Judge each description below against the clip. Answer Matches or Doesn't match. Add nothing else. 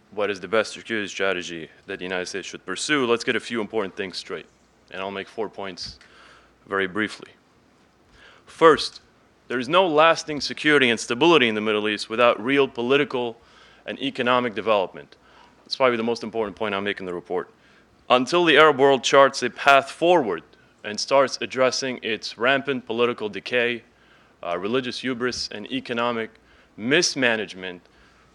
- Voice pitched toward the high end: Doesn't match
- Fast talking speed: Doesn't match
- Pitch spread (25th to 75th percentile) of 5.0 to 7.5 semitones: Doesn't match